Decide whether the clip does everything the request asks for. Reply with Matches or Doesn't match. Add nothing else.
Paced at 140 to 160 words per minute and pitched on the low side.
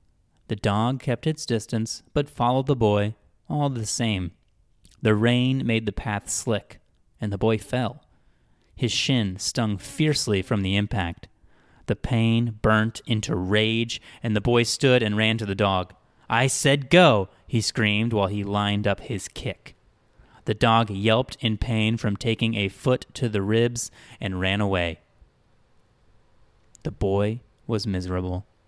Matches